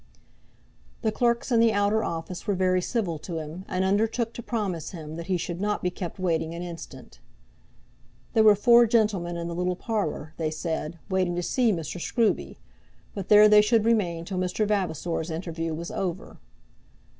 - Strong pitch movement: No, average, 4.0 semitones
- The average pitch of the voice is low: No, medium, 185 Hz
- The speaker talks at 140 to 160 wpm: No, average, 180 wpm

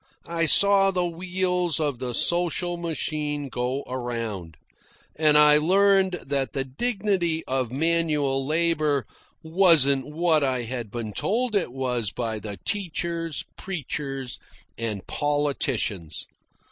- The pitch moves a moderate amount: Yes, average, 5.0 semitones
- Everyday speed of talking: No, slow, 120 wpm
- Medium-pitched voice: Yes, medium, 150 Hz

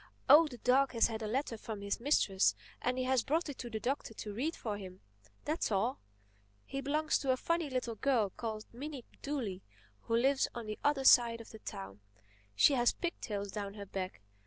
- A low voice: No, high, 240 Hz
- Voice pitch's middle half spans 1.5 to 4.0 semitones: No, average, 4.5 semitones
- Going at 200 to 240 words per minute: Yes, fast, 205 wpm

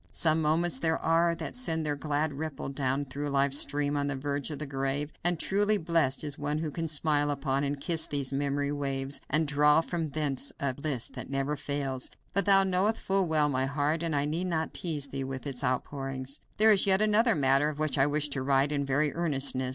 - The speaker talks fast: Yes, fast, 220 wpm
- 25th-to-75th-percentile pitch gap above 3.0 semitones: No, average, 2.7 semitones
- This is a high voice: No, medium, 145 Hz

